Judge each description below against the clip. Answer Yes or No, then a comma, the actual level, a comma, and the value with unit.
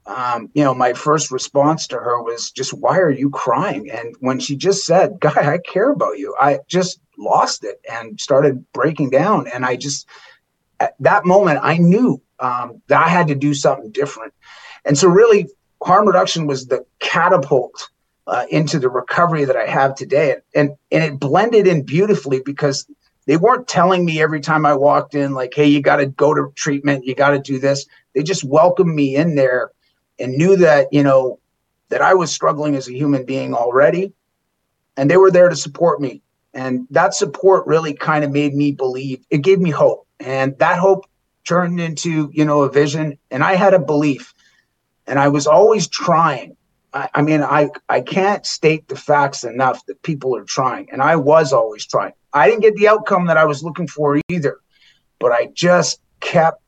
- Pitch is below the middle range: No, medium, 150 Hz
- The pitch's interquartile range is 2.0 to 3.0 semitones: No, average, 4.2 semitones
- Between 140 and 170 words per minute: No, average, 200 wpm